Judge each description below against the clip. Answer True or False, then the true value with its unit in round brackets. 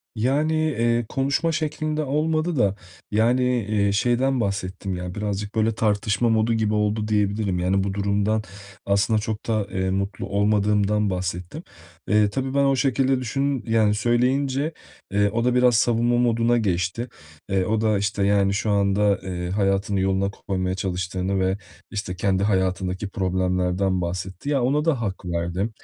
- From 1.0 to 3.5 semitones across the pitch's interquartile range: False (3.9 semitones)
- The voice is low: True (105 Hz)